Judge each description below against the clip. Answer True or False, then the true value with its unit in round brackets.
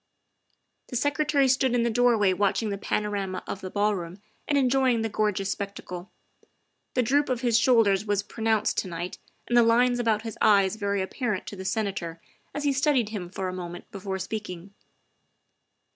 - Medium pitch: False (210 Hz)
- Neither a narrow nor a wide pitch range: True (4.1 semitones)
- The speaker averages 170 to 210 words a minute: True (175 wpm)